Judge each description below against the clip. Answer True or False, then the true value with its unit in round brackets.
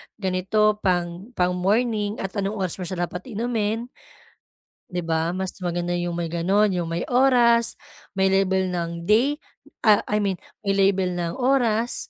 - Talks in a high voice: True (195 Hz)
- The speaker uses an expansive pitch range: False (3.5 semitones)